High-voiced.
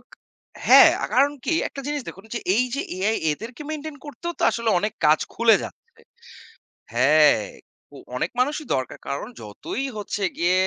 Yes: high, 225 Hz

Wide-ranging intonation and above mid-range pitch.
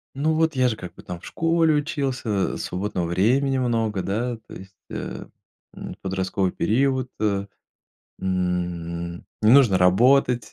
No: wide, 6.4 semitones; low, 110 Hz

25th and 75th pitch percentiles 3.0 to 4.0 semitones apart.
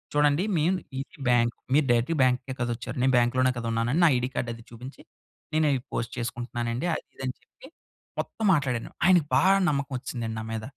Yes: average, 3.7 semitones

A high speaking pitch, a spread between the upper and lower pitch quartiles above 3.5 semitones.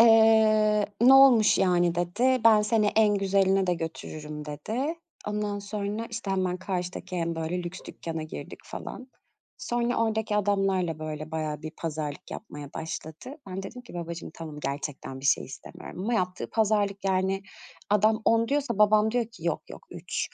Yes: high, 195 Hz; average, 4.8 semitones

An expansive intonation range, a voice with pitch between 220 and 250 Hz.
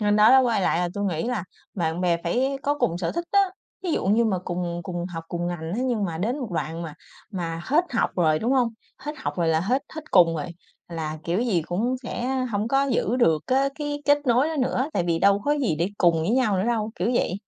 No: wide, 6.8 semitones; high, 200 Hz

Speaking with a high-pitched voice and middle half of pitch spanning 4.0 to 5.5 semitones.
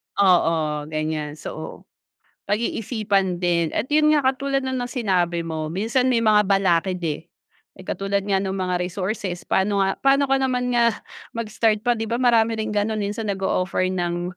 Yes: high, 200 Hz; average, 4.5 semitones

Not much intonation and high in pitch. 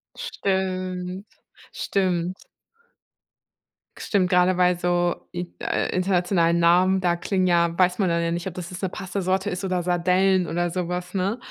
No: narrow, 1.2 semitones; medium, 180 Hz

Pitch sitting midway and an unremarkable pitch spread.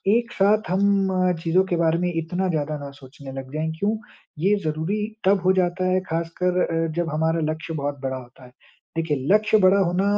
Yes: medium, 175 Hz; average, 3.5 semitones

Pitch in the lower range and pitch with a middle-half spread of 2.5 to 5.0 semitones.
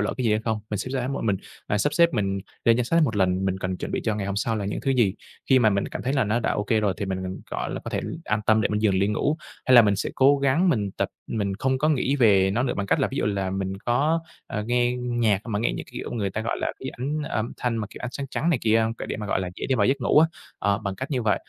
Yes: low, 110 Hz; average, 4.5 semitones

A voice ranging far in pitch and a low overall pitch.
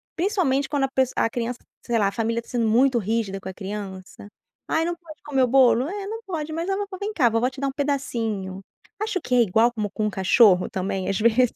No: wide, 5.8 semitones; high, 245 Hz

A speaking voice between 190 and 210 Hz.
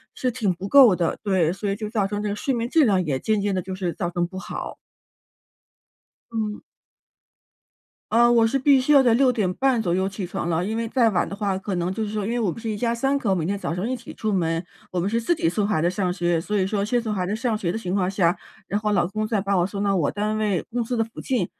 Yes: high, 205 Hz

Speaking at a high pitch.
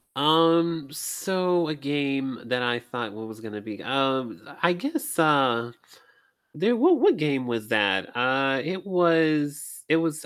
No: medium, 140 Hz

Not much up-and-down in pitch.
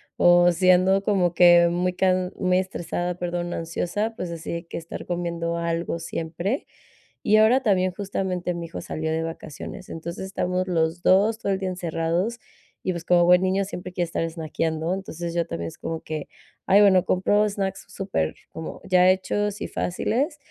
Yes: narrow, 2.2 semitones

